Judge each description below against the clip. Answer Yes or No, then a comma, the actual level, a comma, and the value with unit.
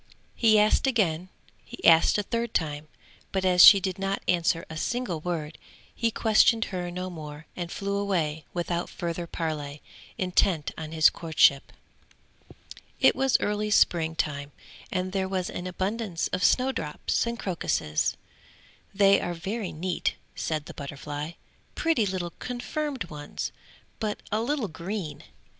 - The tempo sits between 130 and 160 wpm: Yes, average, 145 wpm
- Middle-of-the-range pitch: Yes, medium, 180 Hz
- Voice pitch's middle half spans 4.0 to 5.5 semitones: Yes, average, 4.6 semitones